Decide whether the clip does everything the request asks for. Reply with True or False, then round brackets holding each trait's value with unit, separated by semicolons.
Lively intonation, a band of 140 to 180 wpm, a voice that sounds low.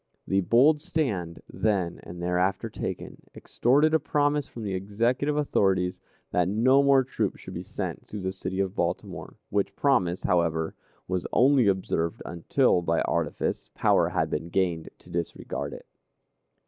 True (6.8 semitones; 150 wpm; 100 Hz)